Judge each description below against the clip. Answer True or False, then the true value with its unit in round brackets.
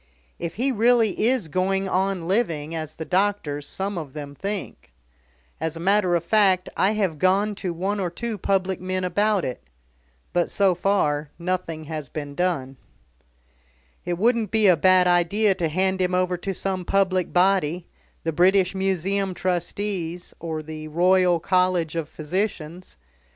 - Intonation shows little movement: False (3.0 semitones)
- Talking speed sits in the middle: True (155 wpm)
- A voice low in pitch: False (185 Hz)